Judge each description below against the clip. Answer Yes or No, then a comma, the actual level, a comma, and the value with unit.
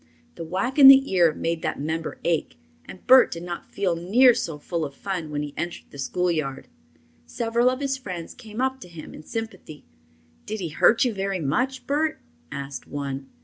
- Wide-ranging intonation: Yes, wide, 7.5 semitones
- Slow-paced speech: No, average, 190 wpm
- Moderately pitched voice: Yes, medium, 180 Hz